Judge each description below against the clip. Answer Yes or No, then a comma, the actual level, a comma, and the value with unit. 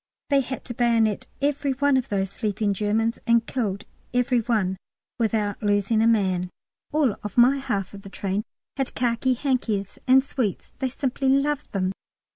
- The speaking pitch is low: No, high, 230 Hz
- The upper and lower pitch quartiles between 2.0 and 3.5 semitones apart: No, average, 4.3 semitones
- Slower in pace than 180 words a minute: Yes, average, 160 wpm